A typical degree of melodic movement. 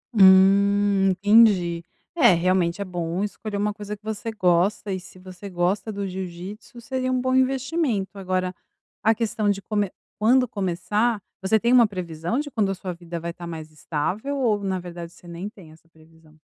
Yes: average, 3.5 semitones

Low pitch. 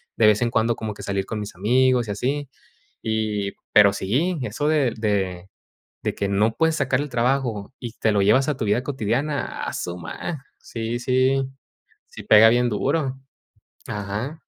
Yes: low, 115 Hz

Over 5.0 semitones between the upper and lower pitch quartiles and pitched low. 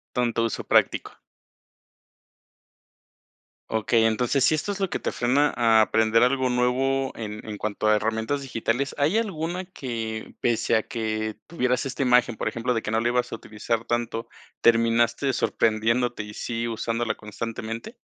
No: narrow, 2.4 semitones; low, 115 Hz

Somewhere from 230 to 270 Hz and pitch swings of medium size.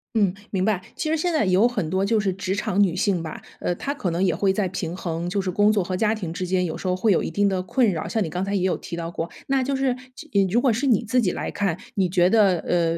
No: high, 195 Hz; average, 3.5 semitones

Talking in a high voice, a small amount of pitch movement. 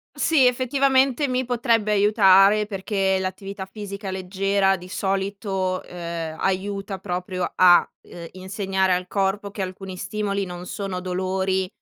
Yes: high, 195 Hz; narrow, 1.8 semitones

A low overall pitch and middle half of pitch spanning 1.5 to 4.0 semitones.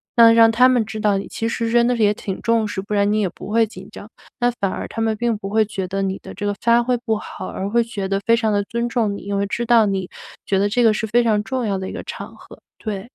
No: high, 215 Hz; narrow, 2.5 semitones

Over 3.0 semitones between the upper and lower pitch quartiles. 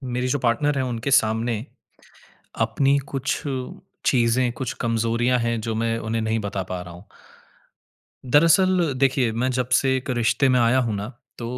No: narrow, 2.6 semitones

